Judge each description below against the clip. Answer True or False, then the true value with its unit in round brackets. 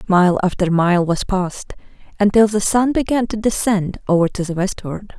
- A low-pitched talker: False (195 Hz)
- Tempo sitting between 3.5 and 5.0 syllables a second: True (4.9 syllables/s)